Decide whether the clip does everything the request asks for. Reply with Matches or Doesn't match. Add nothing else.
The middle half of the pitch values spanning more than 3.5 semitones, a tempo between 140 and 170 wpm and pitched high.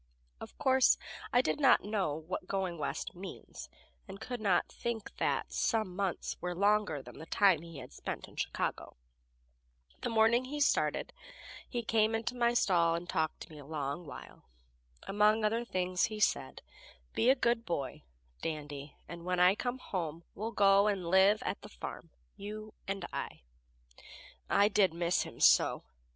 Matches